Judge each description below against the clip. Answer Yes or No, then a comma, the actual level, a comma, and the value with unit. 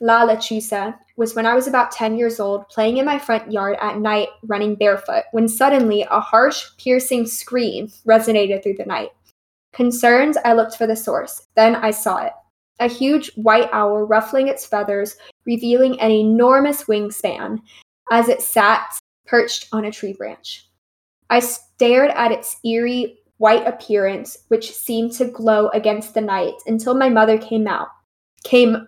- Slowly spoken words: No, average, 165 wpm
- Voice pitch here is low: No, high, 225 Hz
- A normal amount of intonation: No, narrow, 2.1 semitones